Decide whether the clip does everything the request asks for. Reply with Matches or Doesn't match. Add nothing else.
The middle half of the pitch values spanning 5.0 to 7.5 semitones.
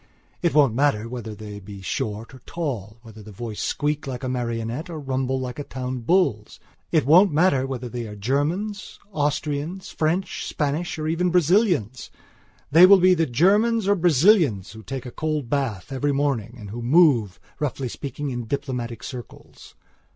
Matches